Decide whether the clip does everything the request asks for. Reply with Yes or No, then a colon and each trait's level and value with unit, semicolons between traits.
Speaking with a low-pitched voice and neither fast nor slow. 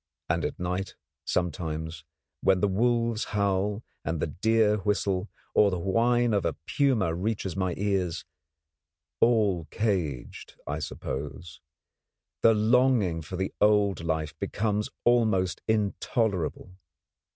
No: very low, 95 Hz; slow, 120 wpm